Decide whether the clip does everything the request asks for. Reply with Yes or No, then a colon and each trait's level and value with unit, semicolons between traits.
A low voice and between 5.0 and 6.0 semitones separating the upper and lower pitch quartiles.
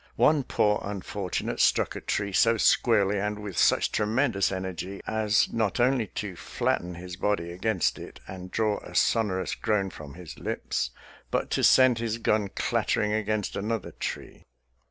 No: low, 105 Hz; average, 2.8 semitones